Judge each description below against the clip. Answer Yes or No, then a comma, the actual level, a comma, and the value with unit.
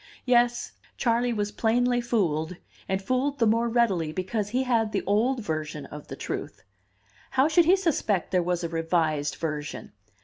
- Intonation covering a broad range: Yes, wide, 6.5 semitones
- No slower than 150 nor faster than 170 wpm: Yes, average, 165 wpm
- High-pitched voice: Yes, high, 215 Hz